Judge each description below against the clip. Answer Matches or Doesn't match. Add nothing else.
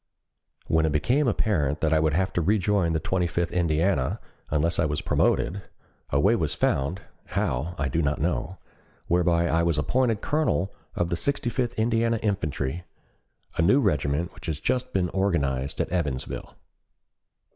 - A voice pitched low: Matches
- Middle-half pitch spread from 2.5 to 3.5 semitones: Doesn't match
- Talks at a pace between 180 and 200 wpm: Doesn't match